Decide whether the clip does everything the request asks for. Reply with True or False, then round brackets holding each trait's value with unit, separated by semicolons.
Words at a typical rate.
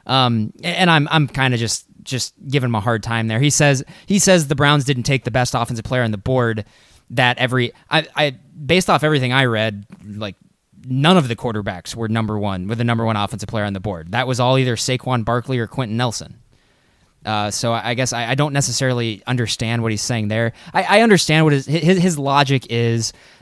False (220 wpm)